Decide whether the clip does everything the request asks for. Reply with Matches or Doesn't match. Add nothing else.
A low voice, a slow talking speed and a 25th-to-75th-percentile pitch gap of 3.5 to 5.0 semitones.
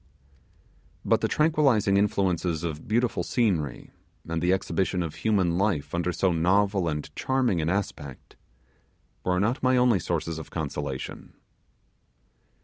Matches